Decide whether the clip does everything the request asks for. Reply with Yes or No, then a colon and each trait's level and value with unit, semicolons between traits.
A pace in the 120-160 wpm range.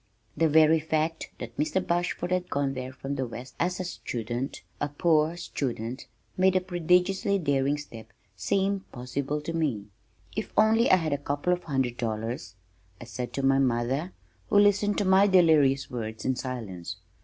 No: average, 170 wpm